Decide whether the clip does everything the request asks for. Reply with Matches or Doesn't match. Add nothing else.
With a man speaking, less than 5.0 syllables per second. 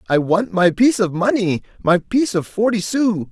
Doesn't match